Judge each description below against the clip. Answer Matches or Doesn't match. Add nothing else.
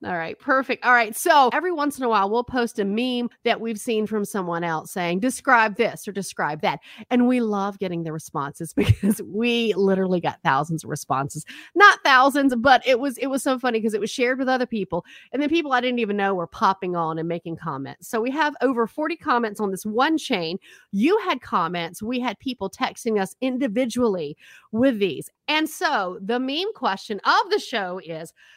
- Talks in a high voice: Matches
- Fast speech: Matches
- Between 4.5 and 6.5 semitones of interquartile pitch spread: Matches